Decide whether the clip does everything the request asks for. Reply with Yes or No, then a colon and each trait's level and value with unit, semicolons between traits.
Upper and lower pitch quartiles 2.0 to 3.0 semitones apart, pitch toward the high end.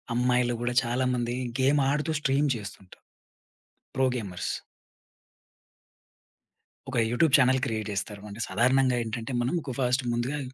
No: narrow, 2.4 semitones; low, 125 Hz